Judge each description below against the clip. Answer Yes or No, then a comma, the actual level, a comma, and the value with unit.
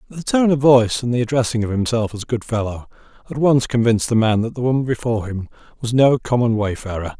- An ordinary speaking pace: No, fast, 215 wpm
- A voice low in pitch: Yes, low, 120 Hz